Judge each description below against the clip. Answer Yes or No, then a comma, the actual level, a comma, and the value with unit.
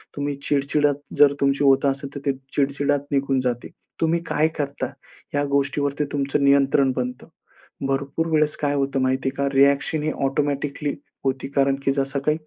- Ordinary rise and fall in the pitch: No, narrow, 1.0 semitones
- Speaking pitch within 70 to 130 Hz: No, medium, 140 Hz